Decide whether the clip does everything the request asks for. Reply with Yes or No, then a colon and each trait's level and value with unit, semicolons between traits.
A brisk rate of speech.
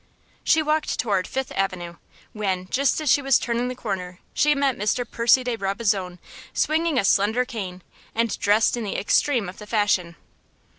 No: average, 170 wpm